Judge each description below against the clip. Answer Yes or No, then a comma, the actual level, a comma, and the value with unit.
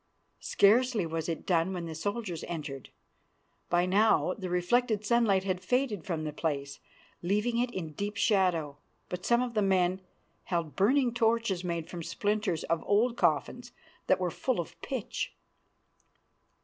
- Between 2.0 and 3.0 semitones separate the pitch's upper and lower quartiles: No, average, 4.6 semitones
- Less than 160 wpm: Yes, average, 150 wpm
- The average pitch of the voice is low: No, high, 190 Hz